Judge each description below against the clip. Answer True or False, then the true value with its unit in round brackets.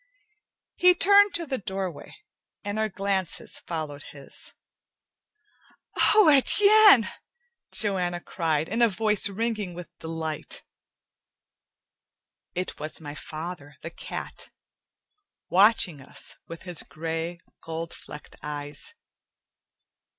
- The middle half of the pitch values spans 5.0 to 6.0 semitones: True (5.4 semitones)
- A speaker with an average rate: False (100 wpm)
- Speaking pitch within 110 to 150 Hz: False (180 Hz)